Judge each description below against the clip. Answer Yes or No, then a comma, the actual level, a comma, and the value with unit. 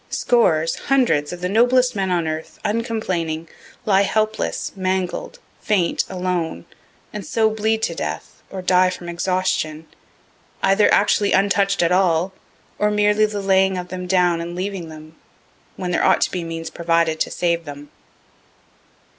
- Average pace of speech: Yes, average, 150 wpm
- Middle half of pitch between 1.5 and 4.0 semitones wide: Yes, average, 3.4 semitones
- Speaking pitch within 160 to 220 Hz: Yes, medium, 185 Hz